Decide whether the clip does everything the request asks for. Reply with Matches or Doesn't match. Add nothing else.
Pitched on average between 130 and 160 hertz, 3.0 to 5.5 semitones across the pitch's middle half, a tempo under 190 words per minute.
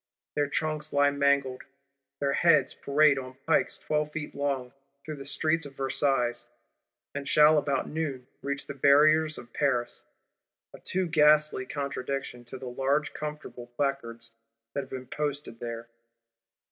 Doesn't match